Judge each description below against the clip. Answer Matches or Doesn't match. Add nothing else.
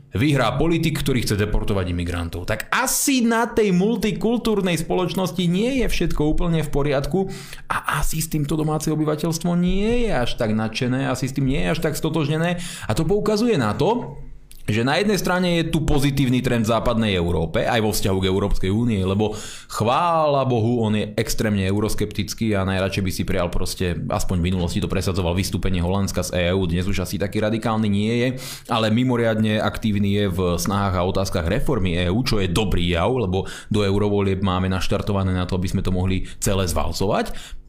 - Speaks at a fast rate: Matches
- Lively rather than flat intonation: Matches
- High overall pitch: Doesn't match